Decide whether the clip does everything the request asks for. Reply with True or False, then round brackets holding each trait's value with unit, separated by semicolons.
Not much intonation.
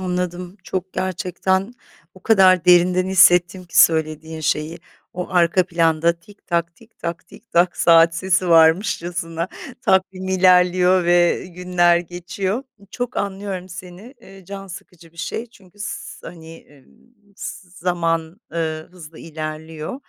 True (2.1 semitones)